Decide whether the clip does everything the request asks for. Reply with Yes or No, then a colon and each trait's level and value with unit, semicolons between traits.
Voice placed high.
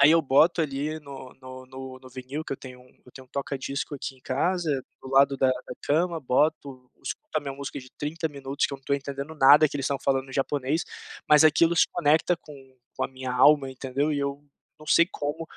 No: medium, 140 Hz